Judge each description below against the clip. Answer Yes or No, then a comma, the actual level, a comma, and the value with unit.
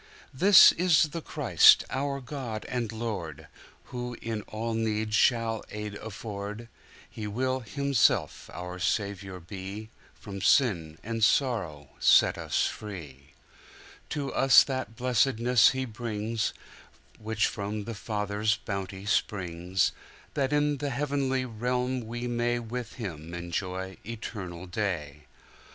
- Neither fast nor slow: No, slow, 105 wpm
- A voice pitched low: Yes, low, 110 Hz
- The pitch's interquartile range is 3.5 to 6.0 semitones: Yes, average, 4.2 semitones